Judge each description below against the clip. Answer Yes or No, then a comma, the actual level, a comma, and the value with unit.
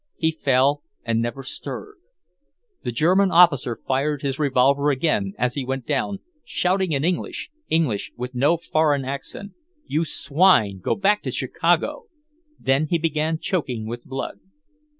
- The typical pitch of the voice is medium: Yes, medium, 145 Hz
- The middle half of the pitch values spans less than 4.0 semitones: No, average, 4.3 semitones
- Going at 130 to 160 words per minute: Yes, average, 145 wpm